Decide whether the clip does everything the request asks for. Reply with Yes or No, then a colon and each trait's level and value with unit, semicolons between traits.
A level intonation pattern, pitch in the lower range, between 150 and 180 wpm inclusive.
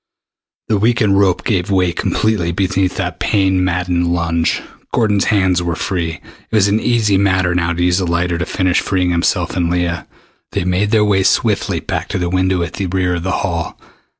No: narrow, 2.1 semitones; very low, 90 Hz; average, 195 wpm